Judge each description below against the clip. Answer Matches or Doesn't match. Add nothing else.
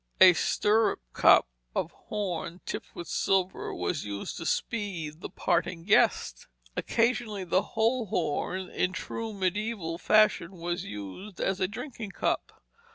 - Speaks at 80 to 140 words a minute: Matches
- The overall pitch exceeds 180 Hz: Matches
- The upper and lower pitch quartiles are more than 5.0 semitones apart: Doesn't match